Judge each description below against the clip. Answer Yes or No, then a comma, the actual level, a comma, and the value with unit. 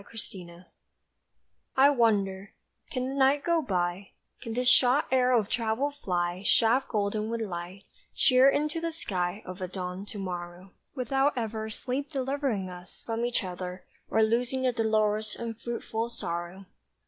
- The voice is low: No, high, 220 Hz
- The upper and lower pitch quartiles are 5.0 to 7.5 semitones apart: Yes, average, 5.3 semitones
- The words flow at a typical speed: Yes, average, 150 wpm